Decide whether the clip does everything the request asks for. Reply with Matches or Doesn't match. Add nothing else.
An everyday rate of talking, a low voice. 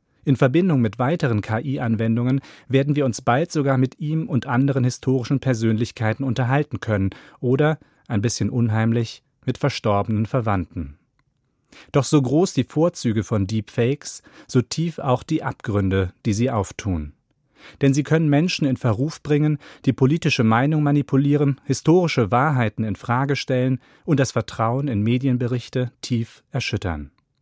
Matches